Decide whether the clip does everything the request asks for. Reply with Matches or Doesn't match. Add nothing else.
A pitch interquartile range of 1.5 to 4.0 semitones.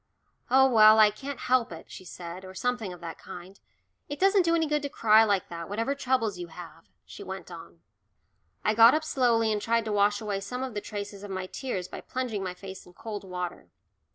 Doesn't match